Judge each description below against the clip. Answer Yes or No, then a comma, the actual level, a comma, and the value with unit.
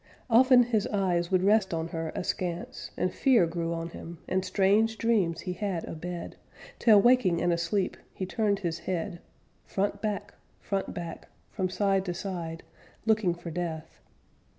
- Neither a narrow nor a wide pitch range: Yes, average, 3.3 semitones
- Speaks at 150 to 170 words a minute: Yes, average, 160 wpm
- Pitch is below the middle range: No, medium, 185 Hz